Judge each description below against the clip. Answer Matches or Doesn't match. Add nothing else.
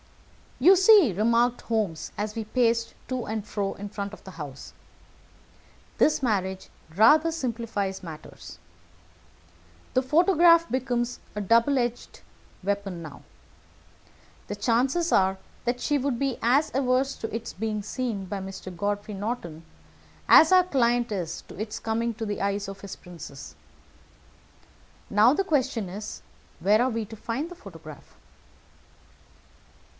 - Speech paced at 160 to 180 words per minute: Doesn't match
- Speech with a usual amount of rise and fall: Matches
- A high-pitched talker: Matches